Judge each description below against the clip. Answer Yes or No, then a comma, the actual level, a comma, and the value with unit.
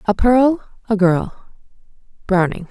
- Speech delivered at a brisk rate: No, slow, 110 wpm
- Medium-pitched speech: No, high, 210 Hz